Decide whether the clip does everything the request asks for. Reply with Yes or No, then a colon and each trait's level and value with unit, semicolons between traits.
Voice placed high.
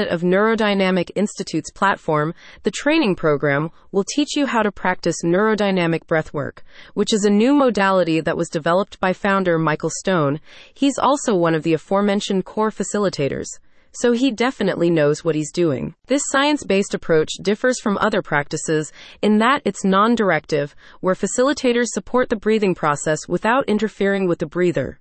Yes: high, 195 Hz